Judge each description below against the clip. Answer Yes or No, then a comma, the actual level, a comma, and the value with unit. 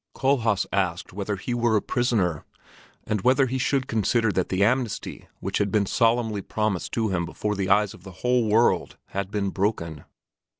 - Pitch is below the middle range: Yes, low, 105 Hz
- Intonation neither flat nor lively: Yes, average, 3.5 semitones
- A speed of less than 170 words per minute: No, average, 180 wpm